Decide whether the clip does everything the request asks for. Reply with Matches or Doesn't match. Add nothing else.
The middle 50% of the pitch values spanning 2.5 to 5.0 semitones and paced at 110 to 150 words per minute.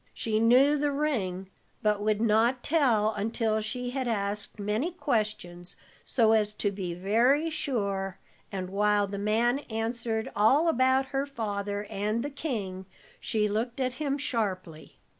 Matches